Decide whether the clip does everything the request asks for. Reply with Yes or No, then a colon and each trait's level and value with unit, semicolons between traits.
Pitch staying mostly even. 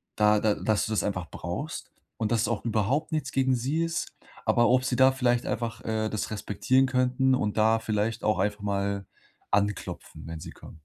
No: average, 3.8 semitones